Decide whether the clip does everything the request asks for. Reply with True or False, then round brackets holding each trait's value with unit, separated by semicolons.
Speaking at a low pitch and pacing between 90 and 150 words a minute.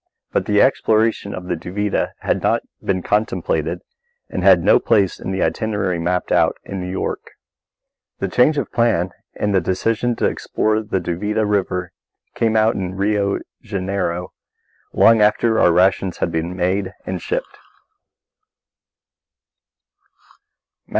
True (100 Hz; 140 wpm)